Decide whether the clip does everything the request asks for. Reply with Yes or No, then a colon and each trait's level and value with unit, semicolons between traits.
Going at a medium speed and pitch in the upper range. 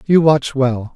No: average, 190 wpm; medium, 140 Hz